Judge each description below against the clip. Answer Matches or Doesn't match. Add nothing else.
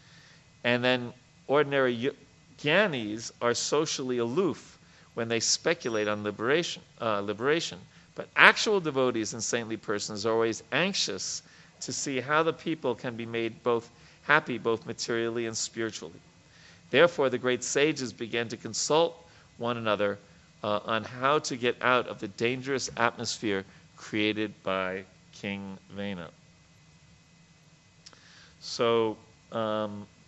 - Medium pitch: Doesn't match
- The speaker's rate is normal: Doesn't match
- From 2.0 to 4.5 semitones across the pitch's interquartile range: Matches